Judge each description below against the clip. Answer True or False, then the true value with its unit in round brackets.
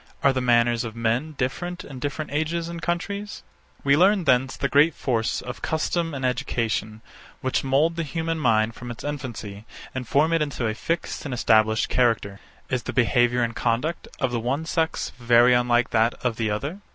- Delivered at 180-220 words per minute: True (190 wpm)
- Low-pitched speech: True (130 Hz)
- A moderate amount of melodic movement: True (4.9 semitones)